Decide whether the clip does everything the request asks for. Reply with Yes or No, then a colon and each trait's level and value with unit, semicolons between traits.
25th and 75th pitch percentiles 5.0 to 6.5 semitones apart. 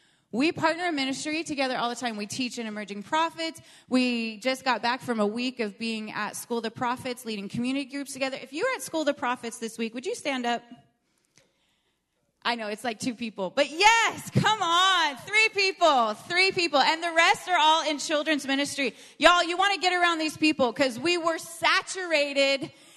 Yes: wide, 5.5 semitones